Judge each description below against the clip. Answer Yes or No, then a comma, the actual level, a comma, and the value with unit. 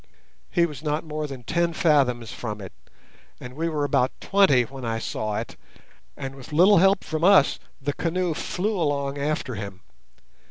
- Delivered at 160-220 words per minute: Yes, average, 170 wpm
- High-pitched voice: No, medium, 145 Hz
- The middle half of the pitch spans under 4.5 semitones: No, average, 4.9 semitones